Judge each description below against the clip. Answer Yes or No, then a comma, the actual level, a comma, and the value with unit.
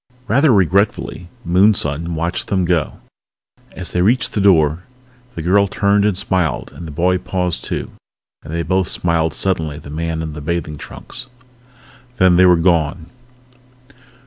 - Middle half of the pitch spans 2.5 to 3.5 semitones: Yes, average, 2.8 semitones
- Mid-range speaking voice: No, very low, 90 Hz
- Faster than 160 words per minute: No, average, 155 wpm